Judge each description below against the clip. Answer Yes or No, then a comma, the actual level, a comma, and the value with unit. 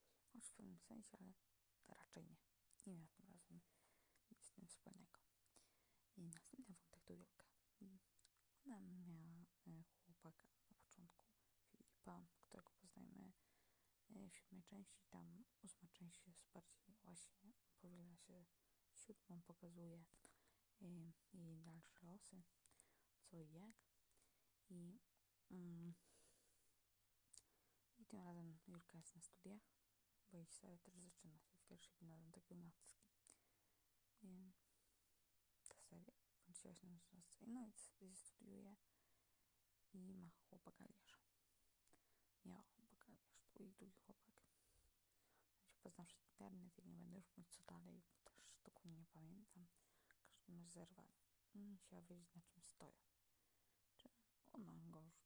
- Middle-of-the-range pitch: Yes, medium, 170 Hz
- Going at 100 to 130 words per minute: Yes, average, 125 wpm